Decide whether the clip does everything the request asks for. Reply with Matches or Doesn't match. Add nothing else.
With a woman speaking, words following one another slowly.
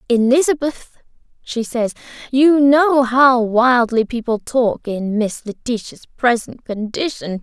Matches